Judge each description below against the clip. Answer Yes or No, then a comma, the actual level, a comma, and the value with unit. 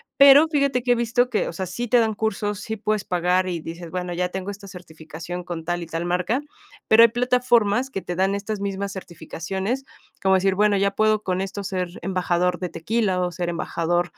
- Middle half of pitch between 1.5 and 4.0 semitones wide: Yes, average, 3.6 semitones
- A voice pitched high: Yes, high, 195 Hz